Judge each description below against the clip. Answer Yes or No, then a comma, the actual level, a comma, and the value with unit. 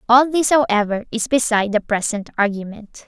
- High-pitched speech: Yes, high, 225 Hz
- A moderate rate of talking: Yes, average, 155 wpm